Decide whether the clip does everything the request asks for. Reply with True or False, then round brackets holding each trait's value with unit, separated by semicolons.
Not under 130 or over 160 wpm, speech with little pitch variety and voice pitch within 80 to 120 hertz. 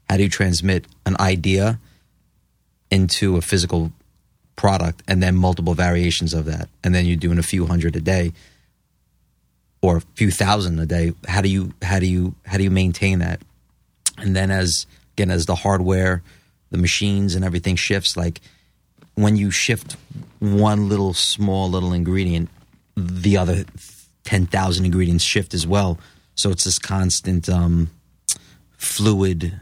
True (155 wpm; 2.1 semitones; 90 Hz)